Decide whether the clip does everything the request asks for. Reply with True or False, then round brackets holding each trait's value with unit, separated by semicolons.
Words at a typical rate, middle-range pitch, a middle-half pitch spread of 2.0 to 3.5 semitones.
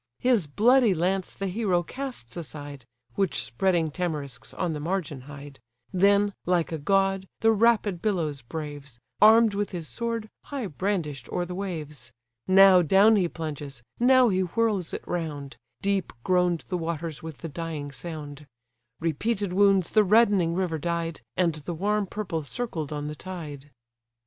False (155 wpm; 175 Hz; 4.8 semitones)